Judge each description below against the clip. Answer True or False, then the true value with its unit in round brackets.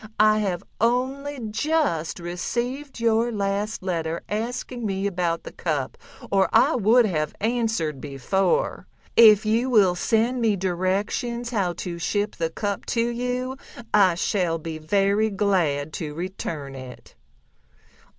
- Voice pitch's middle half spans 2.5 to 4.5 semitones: False (5.2 semitones)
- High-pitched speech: True (200 Hz)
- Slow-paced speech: True (130 wpm)